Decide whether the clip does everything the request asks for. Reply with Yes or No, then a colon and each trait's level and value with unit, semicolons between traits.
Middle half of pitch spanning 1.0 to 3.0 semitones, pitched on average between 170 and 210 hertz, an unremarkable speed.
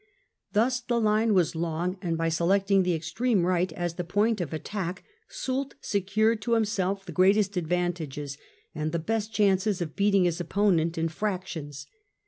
No: average, 3.8 semitones; medium, 185 Hz; average, 160 wpm